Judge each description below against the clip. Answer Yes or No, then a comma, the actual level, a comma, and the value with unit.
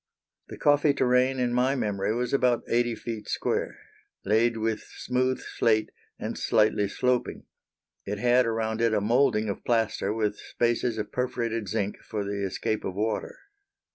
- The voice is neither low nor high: No, low, 115 Hz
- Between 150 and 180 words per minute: Yes, average, 155 wpm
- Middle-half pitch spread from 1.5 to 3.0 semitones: Yes, average, 2.7 semitones